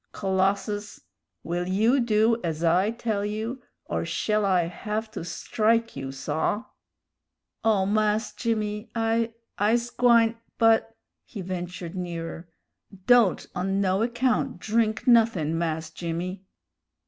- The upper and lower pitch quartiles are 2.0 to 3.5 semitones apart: No, average, 4.0 semitones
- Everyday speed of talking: No, slow, 125 wpm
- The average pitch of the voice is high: Yes, high, 210 Hz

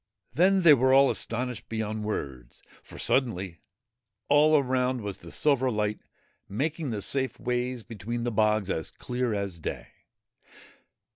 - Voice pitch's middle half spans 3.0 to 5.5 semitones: Yes, average, 3.9 semitones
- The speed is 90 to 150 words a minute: Yes, average, 140 wpm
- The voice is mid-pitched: No, low, 120 Hz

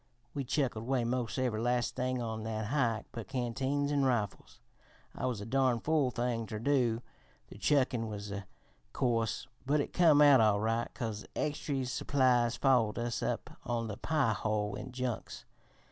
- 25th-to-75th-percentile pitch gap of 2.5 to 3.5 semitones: Yes, average, 3.0 semitones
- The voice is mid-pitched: No, low, 120 Hz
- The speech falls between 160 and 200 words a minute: Yes, average, 170 wpm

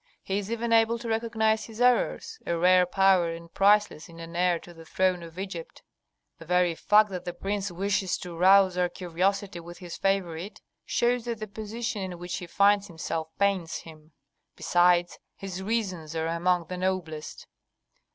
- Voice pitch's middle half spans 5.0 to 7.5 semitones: No, average, 3.1 semitones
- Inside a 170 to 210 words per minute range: Yes, average, 175 wpm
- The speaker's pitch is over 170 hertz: Yes, medium, 185 Hz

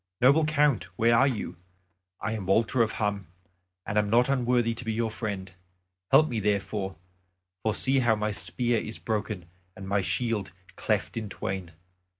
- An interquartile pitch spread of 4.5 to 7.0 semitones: No, average, 3.1 semitones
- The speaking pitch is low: Yes, low, 110 Hz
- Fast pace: No, average, 165 wpm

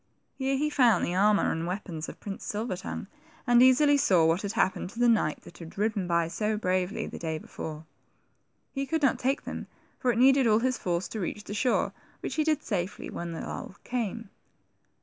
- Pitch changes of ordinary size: No, wide, 6.0 semitones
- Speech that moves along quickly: Yes, fast, 210 wpm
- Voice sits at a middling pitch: No, high, 210 Hz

